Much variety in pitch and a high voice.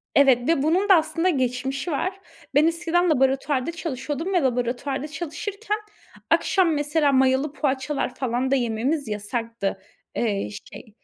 No: average, 4.5 semitones; very high, 280 Hz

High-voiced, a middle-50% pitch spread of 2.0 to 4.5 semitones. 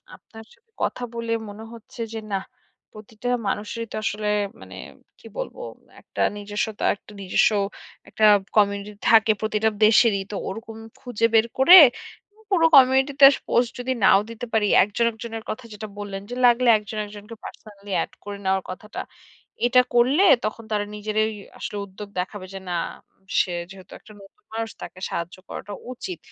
Yes: high, 215 Hz; narrow, 2.4 semitones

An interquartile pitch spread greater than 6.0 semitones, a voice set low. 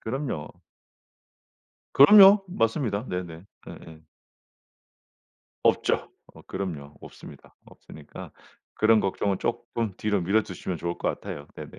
No: average, 5.2 semitones; low, 100 Hz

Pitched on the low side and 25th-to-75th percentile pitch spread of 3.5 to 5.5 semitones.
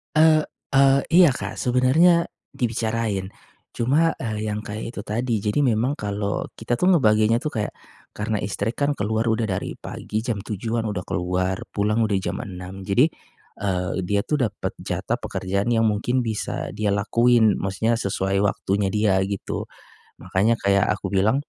No: low, 110 Hz; average, 3.0 semitones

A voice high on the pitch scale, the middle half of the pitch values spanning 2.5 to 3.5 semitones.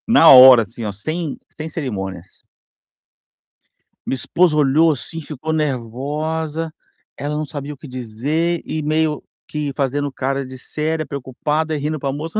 No: medium, 150 Hz; average, 3.2 semitones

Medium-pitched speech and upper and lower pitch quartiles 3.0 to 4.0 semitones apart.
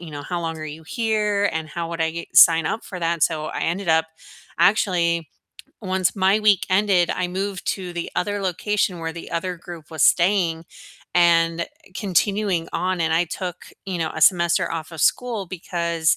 No: medium, 175 Hz; narrow, 2.6 semitones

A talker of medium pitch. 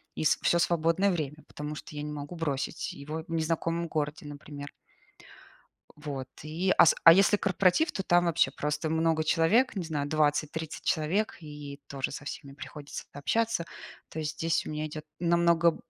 Yes: medium, 155 Hz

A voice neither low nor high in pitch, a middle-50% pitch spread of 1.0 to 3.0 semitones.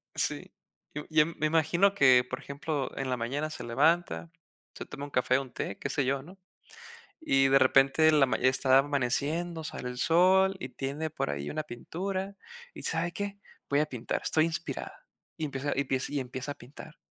No: medium, 145 Hz; average, 3.6 semitones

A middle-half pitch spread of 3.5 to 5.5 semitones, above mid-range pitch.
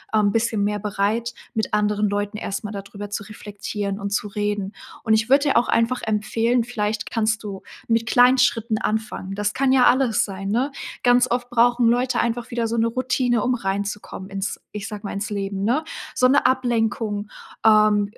No: average, 2.7 semitones; high, 220 Hz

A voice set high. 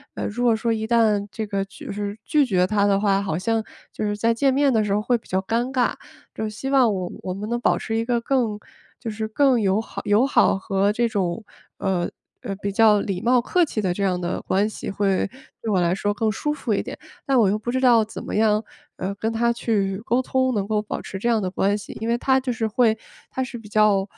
Yes: high, 215 Hz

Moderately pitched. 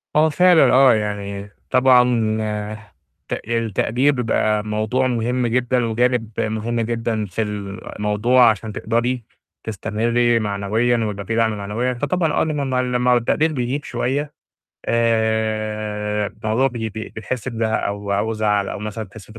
No: low, 115 Hz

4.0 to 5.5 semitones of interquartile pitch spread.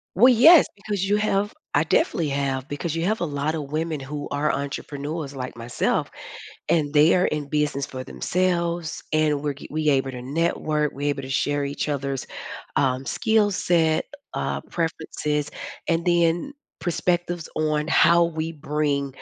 No: average, 3.2 semitones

